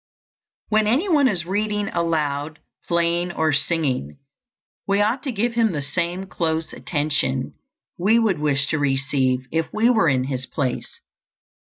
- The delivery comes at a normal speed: Yes, average, 150 wpm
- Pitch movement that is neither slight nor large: No, wide, 6.5 semitones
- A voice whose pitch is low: No, medium, 165 Hz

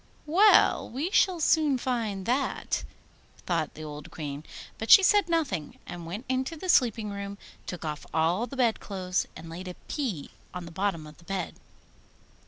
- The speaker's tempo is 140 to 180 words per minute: Yes, average, 175 wpm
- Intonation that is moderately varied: No, wide, 8.1 semitones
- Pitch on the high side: Yes, high, 200 Hz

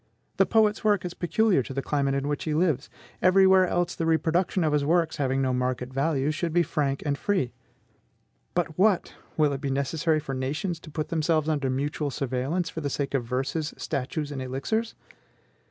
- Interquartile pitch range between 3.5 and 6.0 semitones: Yes, average, 4.0 semitones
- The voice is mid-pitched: Yes, medium, 150 Hz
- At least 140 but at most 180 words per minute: No, average, 195 wpm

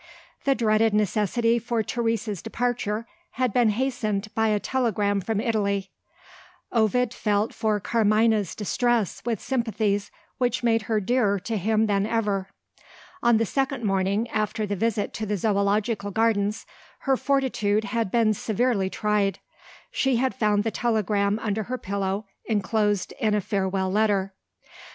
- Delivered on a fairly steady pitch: Yes, narrow, 2.3 semitones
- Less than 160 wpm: Yes, average, 140 wpm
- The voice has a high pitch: Yes, high, 215 Hz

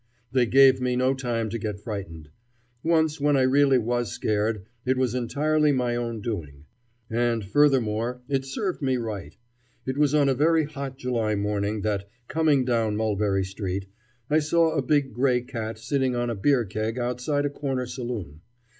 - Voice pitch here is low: Yes, low, 125 Hz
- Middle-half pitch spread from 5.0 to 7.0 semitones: No, average, 4.1 semitones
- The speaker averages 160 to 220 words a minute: Yes, average, 170 wpm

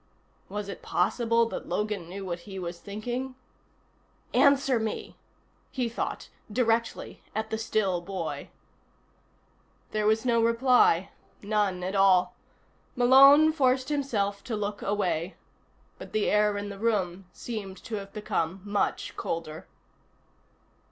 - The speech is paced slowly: Yes, slow, 125 wpm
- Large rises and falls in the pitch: No, average, 3.2 semitones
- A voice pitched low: No, high, 210 Hz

